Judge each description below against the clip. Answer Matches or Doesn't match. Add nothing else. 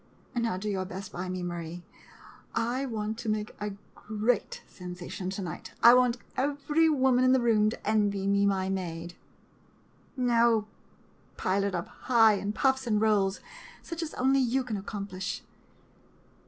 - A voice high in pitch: Matches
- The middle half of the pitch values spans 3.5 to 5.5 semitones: Matches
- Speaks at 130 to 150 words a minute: Doesn't match